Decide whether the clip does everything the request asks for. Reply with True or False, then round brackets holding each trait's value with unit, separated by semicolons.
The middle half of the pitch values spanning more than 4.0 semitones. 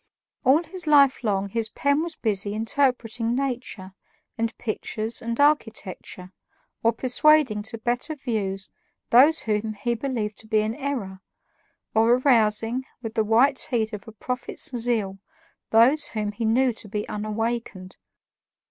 False (3.3 semitones)